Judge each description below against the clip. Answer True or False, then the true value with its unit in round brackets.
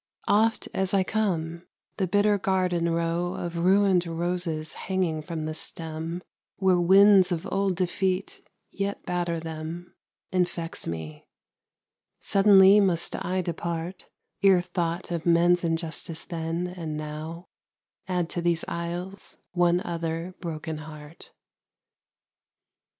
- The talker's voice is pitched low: False (175 Hz)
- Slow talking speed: True (115 wpm)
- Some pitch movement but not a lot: False (2.1 semitones)